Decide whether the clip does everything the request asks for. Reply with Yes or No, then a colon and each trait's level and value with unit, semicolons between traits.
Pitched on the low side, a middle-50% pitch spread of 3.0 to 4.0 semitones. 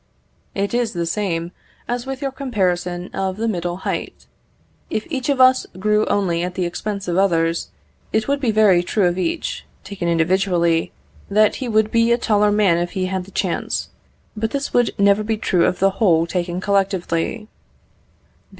No: high, 195 Hz; average, 3.7 semitones